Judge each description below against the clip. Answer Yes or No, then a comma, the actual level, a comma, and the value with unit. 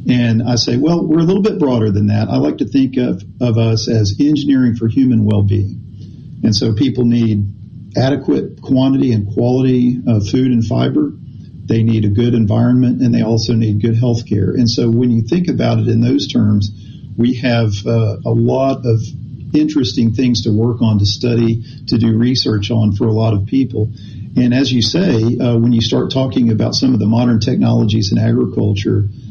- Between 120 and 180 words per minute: No, average, 200 wpm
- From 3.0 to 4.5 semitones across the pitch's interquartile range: No, narrow, 2.4 semitones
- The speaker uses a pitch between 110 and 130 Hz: Yes, low, 115 Hz